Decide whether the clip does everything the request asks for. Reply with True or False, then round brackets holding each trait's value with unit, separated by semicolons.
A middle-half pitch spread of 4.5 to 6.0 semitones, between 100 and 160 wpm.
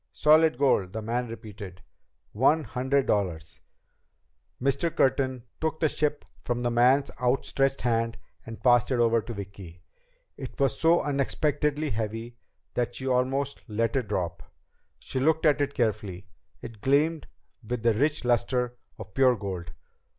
False (4.0 semitones; 145 wpm)